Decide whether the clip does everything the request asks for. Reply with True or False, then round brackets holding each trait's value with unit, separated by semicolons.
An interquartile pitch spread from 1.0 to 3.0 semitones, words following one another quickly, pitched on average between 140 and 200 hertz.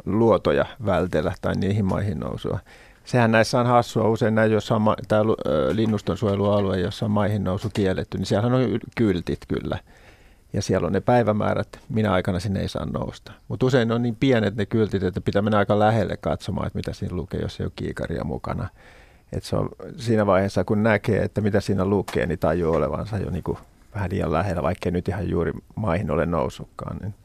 False (2.5 semitones; 190 wpm; 105 Hz)